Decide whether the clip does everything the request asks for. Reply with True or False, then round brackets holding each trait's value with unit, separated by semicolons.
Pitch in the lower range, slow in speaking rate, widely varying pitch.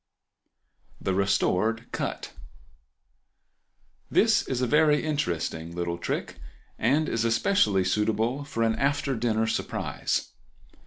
True (110 Hz; 100 wpm; 6.8 semitones)